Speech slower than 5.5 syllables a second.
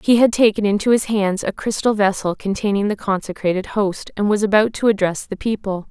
No: 5.6 syllables/s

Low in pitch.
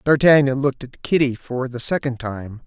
Yes: low, 130 Hz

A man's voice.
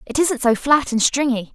No: female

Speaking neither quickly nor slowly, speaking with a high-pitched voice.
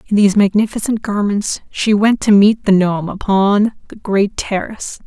Yes: average, 165 wpm; high, 205 Hz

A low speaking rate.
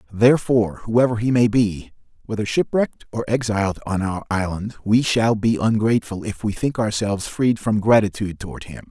No: average, 170 wpm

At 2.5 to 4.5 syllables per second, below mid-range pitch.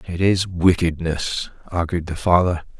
Yes: 4.3 syllables/s; very low, 85 Hz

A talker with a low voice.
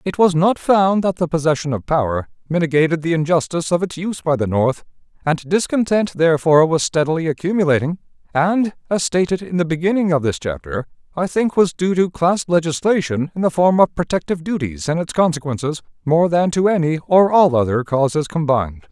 No: medium, 165 Hz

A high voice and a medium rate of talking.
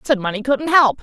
No: very high, 250 Hz; fast, 235 wpm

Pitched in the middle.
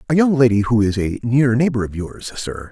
No: low, 115 Hz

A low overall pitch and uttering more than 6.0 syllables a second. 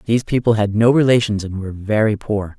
Yes: low, 110 Hz; 6.2 syllables/s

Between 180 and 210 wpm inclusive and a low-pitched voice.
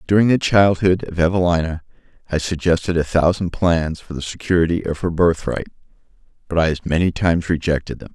No: average, 170 wpm; very low, 85 Hz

